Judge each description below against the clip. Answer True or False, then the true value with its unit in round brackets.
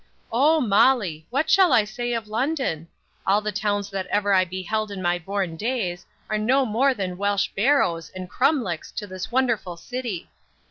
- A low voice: False (210 Hz)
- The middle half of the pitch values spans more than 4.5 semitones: True (4.9 semitones)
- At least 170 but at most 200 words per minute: True (175 wpm)